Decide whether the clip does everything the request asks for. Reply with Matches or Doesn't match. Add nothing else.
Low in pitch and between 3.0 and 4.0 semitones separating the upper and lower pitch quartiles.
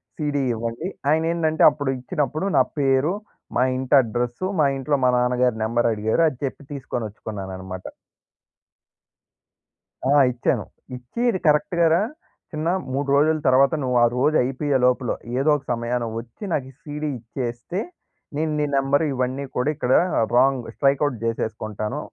Matches